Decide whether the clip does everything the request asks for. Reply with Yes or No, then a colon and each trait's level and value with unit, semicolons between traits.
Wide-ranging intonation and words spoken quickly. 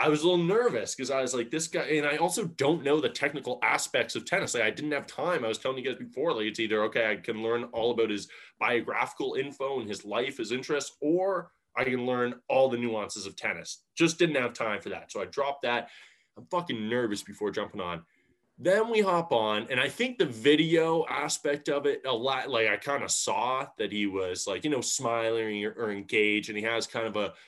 Yes: wide, 6.1 semitones; fast, 240 wpm